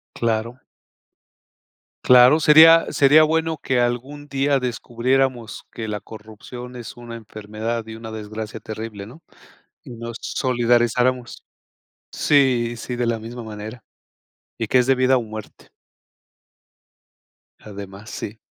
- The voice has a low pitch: Yes, low, 120 Hz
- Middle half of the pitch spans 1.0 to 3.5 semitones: Yes, average, 2.7 semitones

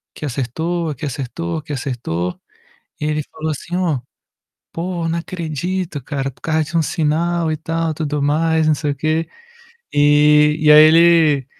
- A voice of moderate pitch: Yes, medium, 155 Hz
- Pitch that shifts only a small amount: Yes, narrow, 2.1 semitones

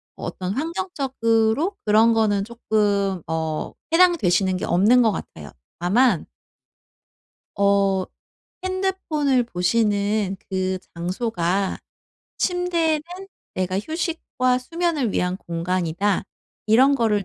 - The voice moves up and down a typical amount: No, wide, 6.6 semitones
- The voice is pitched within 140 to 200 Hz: No, high, 215 Hz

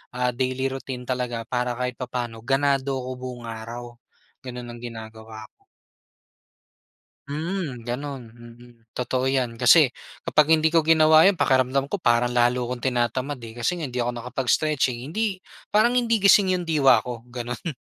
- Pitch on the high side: No, low, 125 Hz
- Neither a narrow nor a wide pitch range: Yes, average, 3.4 semitones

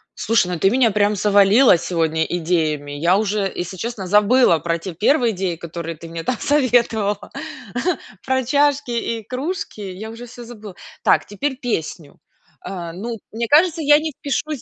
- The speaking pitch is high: Yes, high, 210 Hz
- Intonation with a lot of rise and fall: Yes, wide, 5.9 semitones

